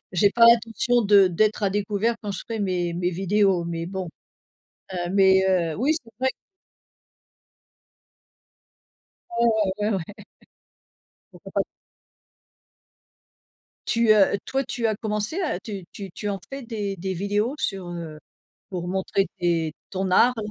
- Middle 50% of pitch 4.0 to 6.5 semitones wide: No, average, 3.2 semitones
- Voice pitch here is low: No, high, 200 Hz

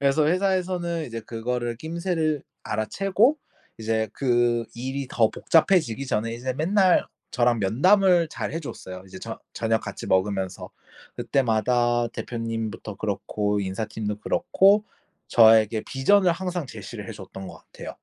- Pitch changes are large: Yes, wide, 7.3 semitones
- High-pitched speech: No, low, 120 Hz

